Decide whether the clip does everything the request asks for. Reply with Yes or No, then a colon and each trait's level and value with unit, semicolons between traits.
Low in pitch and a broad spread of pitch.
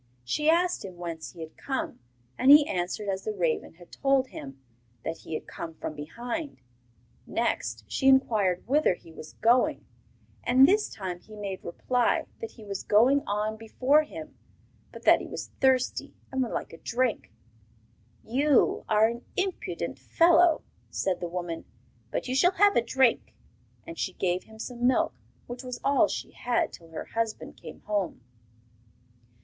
No: high, 225 Hz; wide, 6.9 semitones